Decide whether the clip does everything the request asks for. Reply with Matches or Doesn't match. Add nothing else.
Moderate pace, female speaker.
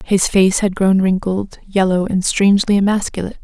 Matches